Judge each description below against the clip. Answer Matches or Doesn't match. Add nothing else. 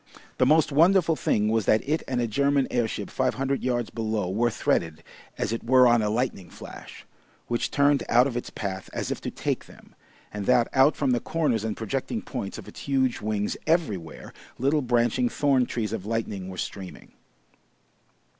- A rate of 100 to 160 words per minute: Doesn't match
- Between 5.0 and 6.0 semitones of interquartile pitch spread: Doesn't match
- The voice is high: Doesn't match